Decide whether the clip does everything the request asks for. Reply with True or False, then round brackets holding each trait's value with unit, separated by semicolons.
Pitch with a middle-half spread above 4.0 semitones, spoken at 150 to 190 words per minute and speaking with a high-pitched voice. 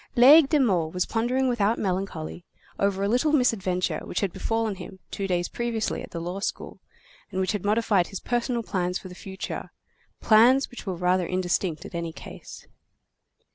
True (4.5 semitones; 175 wpm; 195 Hz)